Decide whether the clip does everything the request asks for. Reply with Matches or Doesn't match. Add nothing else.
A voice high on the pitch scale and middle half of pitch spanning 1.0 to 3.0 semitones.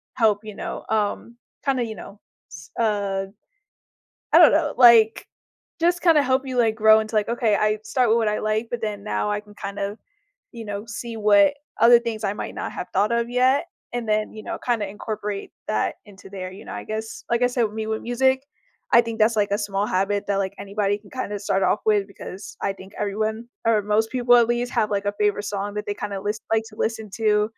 Matches